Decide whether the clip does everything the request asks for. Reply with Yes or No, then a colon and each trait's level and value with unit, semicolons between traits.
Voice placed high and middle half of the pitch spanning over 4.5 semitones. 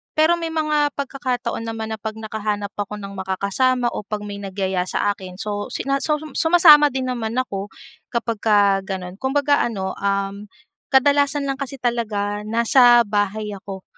Yes: high, 220 Hz; average, 5.0 semitones